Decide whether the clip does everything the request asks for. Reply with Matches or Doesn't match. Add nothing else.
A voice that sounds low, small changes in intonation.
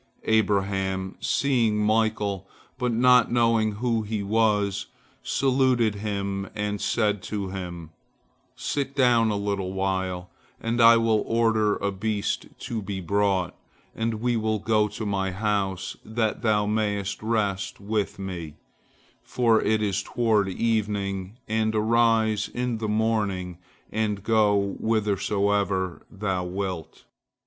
Matches